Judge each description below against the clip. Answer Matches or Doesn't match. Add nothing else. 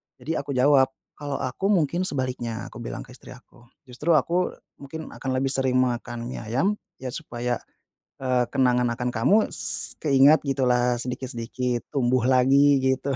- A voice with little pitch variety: Matches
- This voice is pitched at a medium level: Doesn't match